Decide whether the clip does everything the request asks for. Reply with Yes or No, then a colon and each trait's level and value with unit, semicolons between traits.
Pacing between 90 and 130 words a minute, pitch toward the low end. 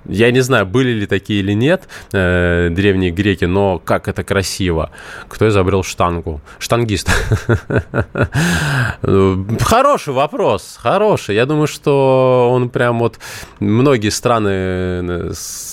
Yes: slow, 110 wpm; low, 100 Hz